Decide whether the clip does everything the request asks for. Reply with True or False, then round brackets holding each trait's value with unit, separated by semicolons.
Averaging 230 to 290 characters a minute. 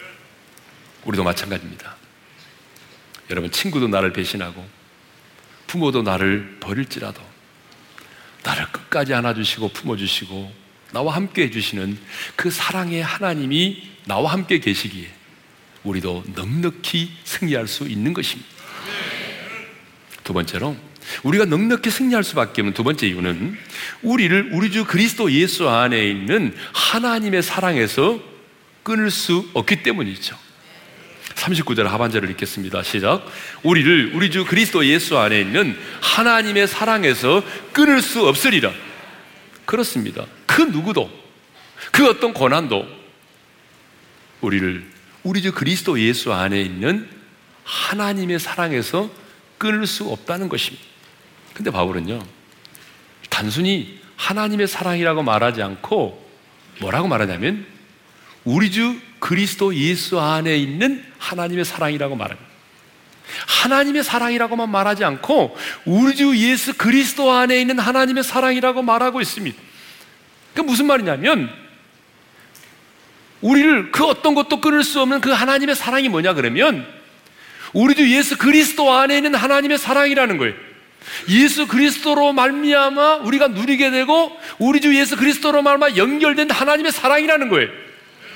False (300 characters per minute)